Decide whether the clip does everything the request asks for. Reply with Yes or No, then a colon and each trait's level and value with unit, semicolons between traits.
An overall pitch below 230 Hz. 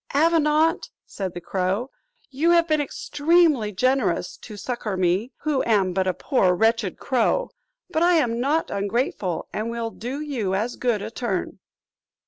No: high, 235 Hz